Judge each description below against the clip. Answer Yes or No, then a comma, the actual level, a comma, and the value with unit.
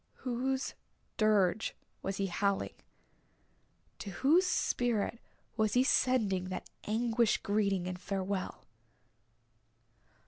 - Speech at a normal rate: No, slow, 95 wpm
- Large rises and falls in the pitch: No, average, 3.8 semitones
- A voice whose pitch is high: Yes, high, 210 Hz